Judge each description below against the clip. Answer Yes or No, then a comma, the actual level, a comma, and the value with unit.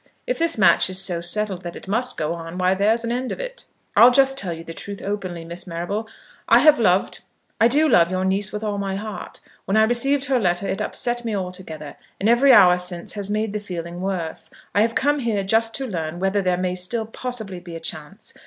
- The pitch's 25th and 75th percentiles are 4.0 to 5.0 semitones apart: Yes, average, 4.5 semitones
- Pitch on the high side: Yes, high, 200 Hz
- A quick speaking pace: Yes, fast, 230 wpm